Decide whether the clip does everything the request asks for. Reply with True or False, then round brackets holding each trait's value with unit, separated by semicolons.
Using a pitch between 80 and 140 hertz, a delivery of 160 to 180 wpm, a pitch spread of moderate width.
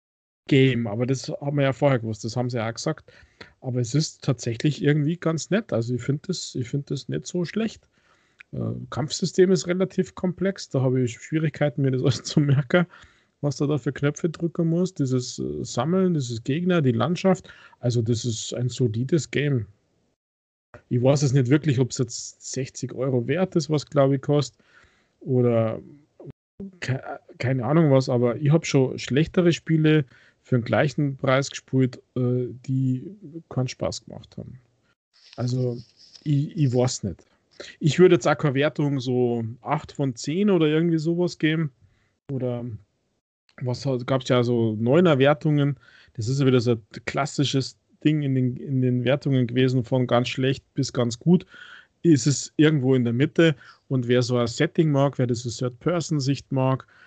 True (135 Hz; 170 wpm; 3.7 semitones)